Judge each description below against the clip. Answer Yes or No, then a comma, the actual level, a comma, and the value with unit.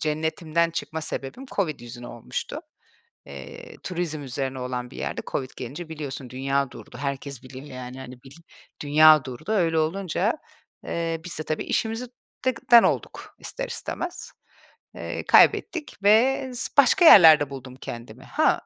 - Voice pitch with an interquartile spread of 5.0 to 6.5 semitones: Yes, wide, 5.5 semitones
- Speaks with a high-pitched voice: No, medium, 155 Hz